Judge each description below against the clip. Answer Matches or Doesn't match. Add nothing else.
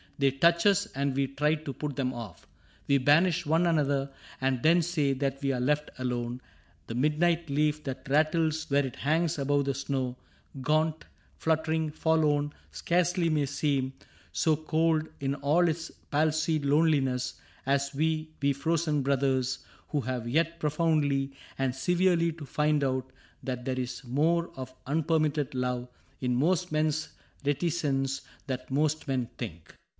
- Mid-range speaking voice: Matches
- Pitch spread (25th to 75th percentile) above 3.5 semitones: Doesn't match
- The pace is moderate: Matches